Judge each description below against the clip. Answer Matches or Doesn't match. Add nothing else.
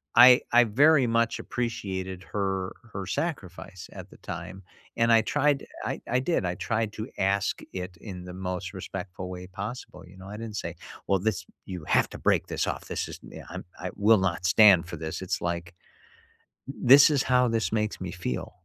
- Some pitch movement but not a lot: Matches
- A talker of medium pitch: Doesn't match